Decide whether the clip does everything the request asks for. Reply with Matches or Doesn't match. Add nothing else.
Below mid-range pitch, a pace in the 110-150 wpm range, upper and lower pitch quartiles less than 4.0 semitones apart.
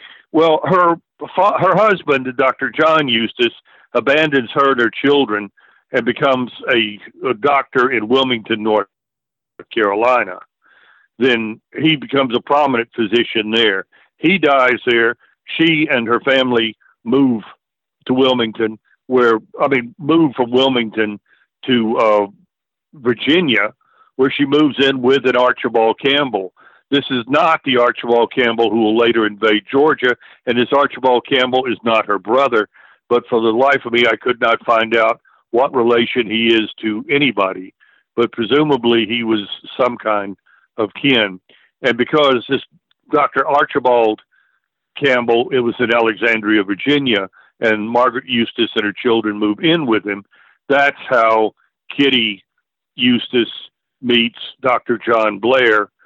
Matches